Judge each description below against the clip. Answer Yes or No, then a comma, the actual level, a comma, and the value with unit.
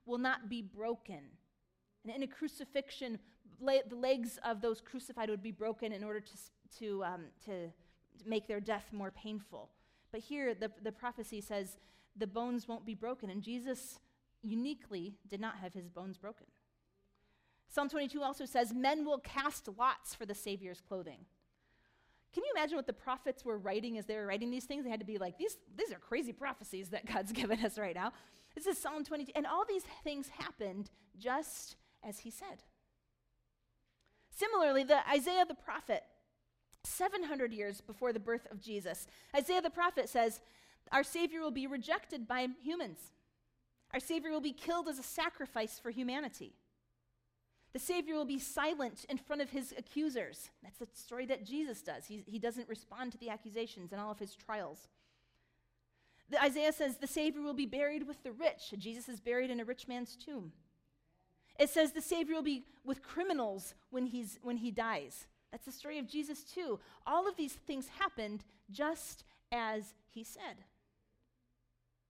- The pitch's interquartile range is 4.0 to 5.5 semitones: Yes, average, 5.2 semitones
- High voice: Yes, high, 240 Hz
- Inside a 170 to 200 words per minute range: Yes, average, 175 wpm